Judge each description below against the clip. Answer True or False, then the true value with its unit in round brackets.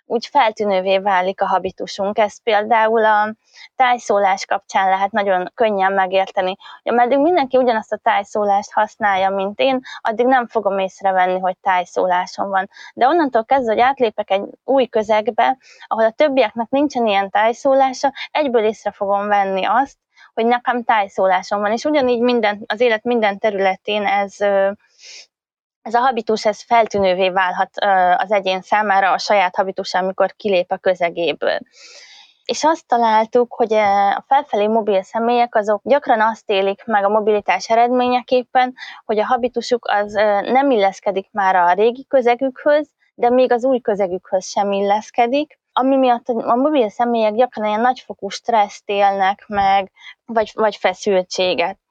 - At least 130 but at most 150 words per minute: True (140 wpm)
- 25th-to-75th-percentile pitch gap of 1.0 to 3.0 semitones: False (3.8 semitones)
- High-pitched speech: True (215 Hz)